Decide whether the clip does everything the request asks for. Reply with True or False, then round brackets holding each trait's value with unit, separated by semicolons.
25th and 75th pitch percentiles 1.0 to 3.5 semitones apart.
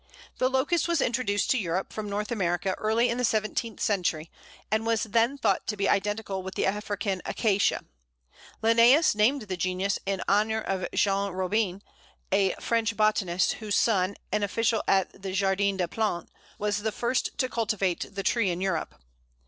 True (2.8 semitones)